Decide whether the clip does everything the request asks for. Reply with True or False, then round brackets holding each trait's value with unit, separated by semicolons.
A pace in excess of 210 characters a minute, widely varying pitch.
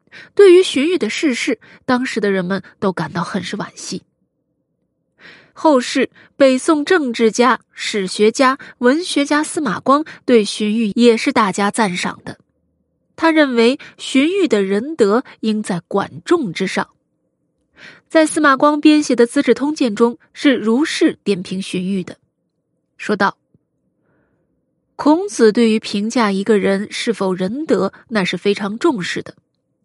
False (205 characters per minute; 6.3 semitones)